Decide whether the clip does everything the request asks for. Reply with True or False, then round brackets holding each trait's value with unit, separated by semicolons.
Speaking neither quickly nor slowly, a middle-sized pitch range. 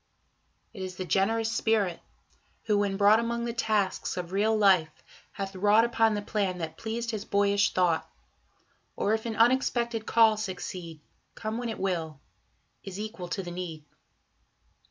True (155 wpm; 3.3 semitones)